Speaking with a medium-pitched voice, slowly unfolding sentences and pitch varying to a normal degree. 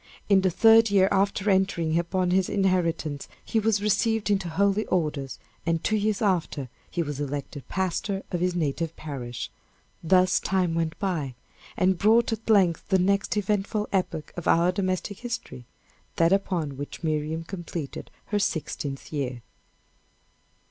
No: medium, 180 Hz; average, 150 wpm; average, 3.8 semitones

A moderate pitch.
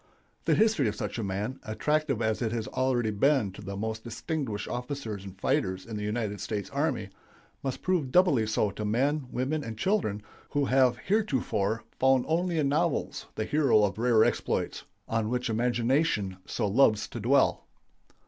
No: low, 120 Hz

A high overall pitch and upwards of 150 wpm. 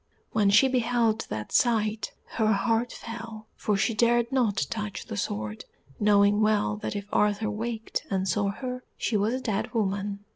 Yes: high, 215 Hz; average, 170 wpm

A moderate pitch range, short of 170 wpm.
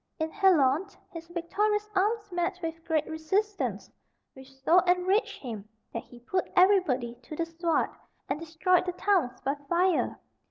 Yes: average, 4.1 semitones; average, 150 wpm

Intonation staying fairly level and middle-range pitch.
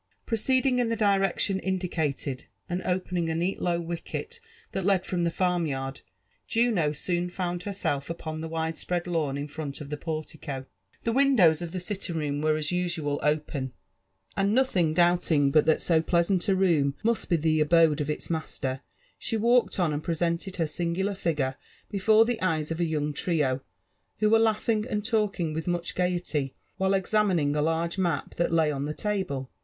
No: average, 4.0 semitones; medium, 170 Hz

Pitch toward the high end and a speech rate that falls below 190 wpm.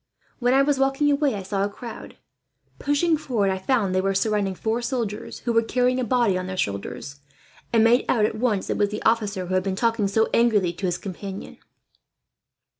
No: high, 215 Hz; fast, 205 wpm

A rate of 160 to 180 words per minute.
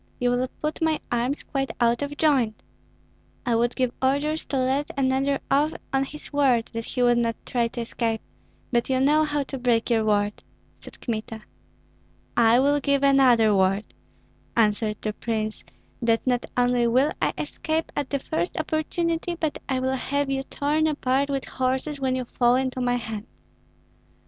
Yes: average, 175 wpm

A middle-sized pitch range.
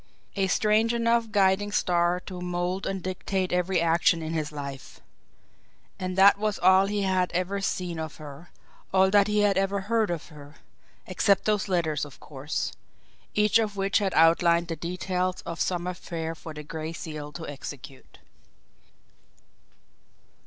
Yes: average, 3.2 semitones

